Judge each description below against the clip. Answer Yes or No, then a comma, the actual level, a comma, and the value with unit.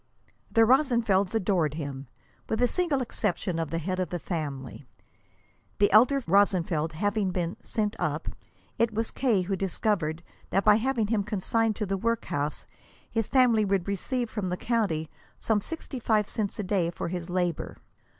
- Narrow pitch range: No, average, 4.4 semitones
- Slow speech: No, average, 165 wpm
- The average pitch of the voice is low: No, high, 200 Hz